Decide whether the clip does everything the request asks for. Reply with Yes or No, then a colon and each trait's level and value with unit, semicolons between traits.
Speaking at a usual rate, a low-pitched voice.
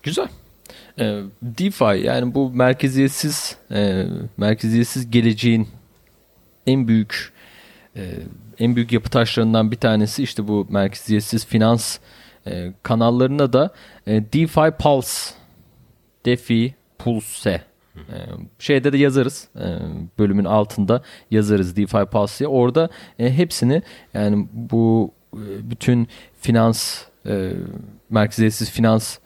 No: slow, 85 wpm; low, 115 Hz